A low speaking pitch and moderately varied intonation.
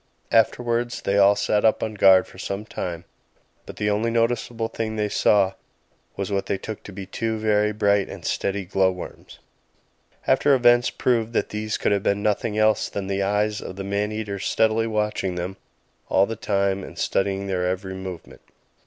No: low, 105 Hz; narrow, 2.0 semitones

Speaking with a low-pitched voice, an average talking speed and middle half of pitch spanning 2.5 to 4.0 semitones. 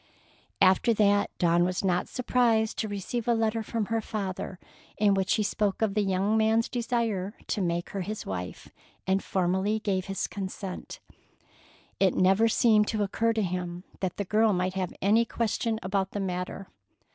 No: high, 200 Hz; average, 170 wpm; average, 2.9 semitones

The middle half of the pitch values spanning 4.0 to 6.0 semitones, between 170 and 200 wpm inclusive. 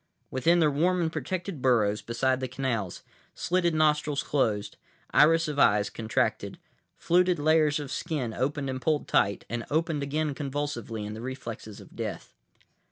No: average, 4.7 semitones; average, 155 wpm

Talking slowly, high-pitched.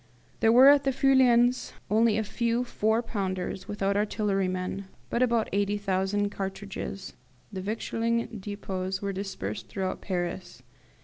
Yes: slow, 125 wpm; high, 205 Hz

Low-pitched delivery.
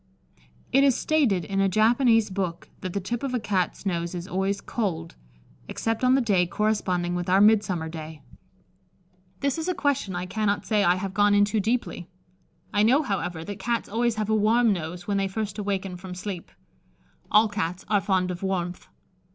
No: high, 200 Hz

